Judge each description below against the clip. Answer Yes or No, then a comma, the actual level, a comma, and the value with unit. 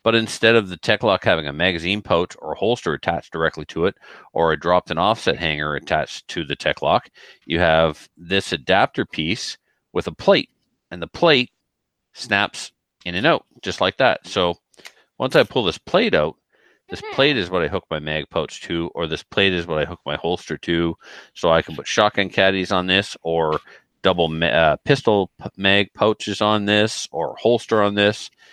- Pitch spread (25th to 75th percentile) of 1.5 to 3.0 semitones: No, average, 3.6 semitones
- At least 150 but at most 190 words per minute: No, average, 200 wpm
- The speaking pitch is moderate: No, very low, 90 Hz